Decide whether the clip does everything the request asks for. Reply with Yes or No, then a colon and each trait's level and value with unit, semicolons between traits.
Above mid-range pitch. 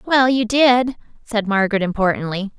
Yes: high, 220 Hz